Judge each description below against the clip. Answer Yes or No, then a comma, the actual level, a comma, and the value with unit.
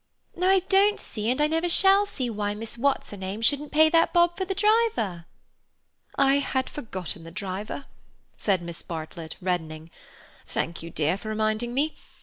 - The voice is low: No, high, 230 Hz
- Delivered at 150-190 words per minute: Yes, average, 175 wpm